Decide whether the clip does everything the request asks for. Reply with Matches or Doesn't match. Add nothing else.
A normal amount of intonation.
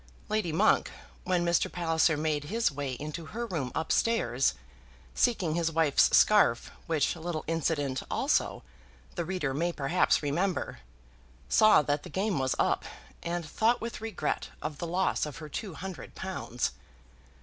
Matches